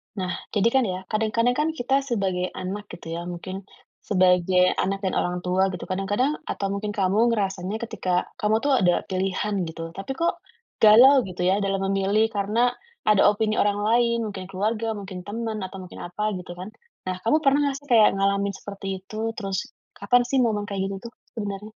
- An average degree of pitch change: Yes, average, 3.2 semitones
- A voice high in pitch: Yes, high, 200 Hz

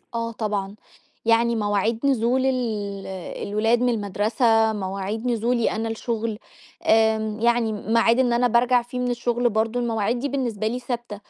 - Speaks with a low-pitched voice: No, high, 230 Hz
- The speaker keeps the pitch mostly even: Yes, narrow, 1.8 semitones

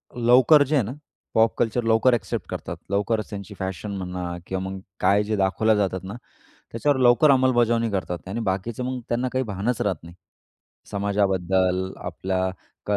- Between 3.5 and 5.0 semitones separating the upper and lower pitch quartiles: Yes, average, 4.1 semitones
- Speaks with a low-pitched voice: Yes, low, 105 Hz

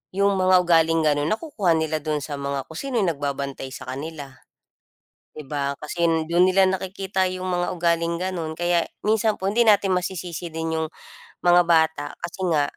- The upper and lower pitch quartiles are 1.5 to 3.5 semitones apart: Yes, average, 3.1 semitones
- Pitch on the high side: No, medium, 170 Hz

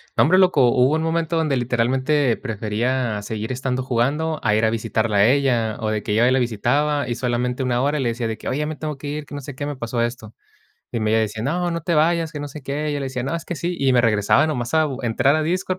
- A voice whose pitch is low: Yes, low, 130 Hz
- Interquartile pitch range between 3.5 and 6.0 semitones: Yes, average, 4.3 semitones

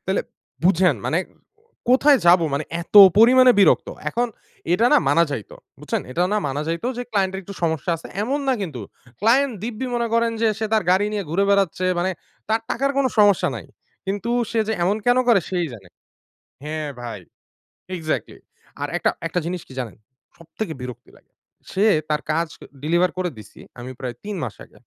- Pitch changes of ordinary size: No, wide, 6.1 semitones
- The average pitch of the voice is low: No, medium, 185 Hz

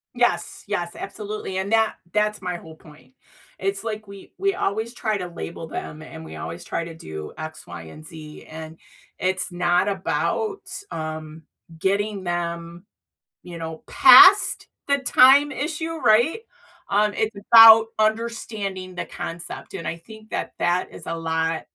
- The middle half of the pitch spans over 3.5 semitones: Yes, average, 4.9 semitones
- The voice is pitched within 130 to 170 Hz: No, high, 190 Hz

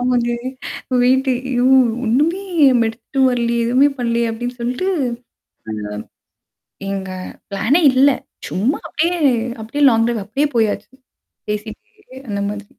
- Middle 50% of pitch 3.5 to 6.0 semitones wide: No, average, 2.9 semitones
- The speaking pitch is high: Yes, high, 240 Hz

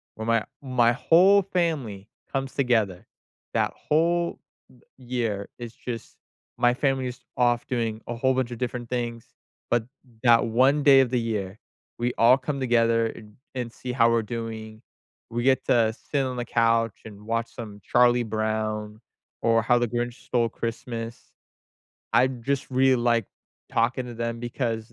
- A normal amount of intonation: No, narrow, 2.0 semitones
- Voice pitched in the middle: No, low, 120 Hz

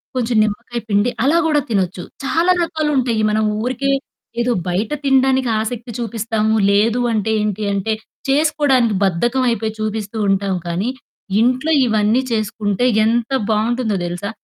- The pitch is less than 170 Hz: No, high, 225 Hz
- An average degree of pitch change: Yes, average, 3.3 semitones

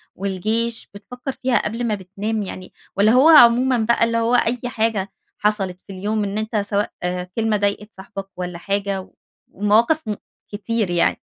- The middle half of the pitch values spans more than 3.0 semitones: No, narrow, 2.6 semitones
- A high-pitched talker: Yes, high, 210 Hz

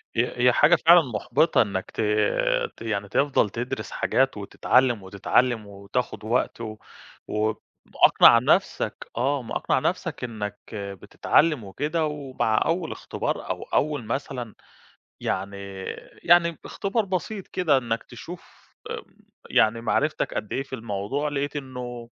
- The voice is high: No, low, 125 Hz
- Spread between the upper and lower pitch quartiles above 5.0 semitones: Yes, wide, 5.6 semitones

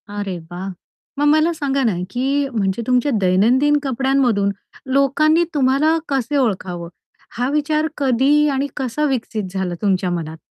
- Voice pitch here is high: Yes, very high, 260 Hz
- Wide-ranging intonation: Yes, wide, 6.1 semitones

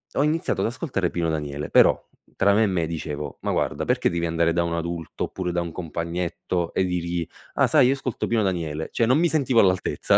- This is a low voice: Yes, very low, 85 Hz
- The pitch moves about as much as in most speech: Yes, average, 4.8 semitones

